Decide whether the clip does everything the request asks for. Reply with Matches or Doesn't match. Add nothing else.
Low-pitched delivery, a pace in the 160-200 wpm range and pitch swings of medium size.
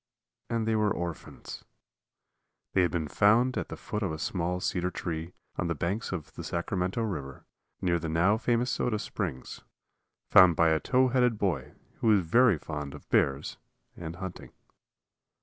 Matches